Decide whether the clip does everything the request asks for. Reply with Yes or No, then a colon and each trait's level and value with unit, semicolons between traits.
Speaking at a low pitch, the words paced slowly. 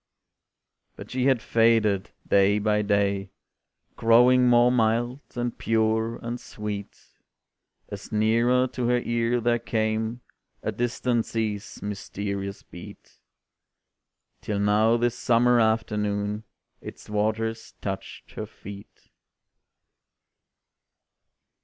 Yes: low, 110 Hz; slow, 100 wpm